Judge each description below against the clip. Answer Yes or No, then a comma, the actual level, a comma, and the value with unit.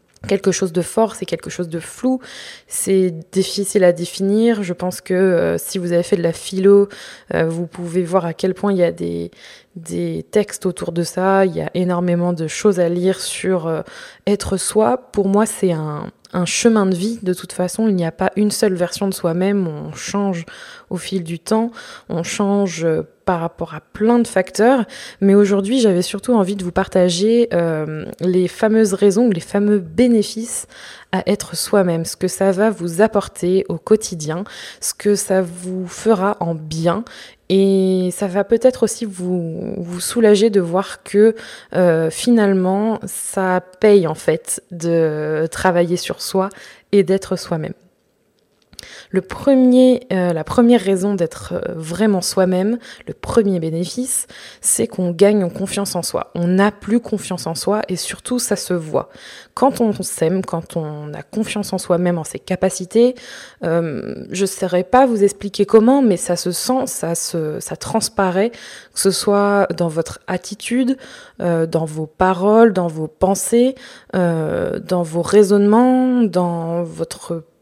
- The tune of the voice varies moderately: Yes, average, 3.3 semitones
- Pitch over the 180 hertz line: Yes, high, 190 Hz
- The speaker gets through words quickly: No, average, 170 wpm